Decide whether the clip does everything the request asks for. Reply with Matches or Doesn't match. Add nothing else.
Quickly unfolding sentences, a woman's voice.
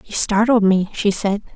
Doesn't match